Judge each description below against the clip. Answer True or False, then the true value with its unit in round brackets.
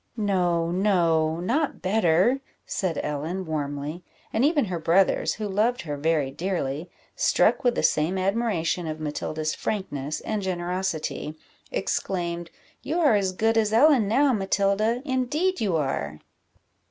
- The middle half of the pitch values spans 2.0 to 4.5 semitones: False (5.6 semitones)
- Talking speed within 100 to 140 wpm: True (135 wpm)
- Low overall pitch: False (185 Hz)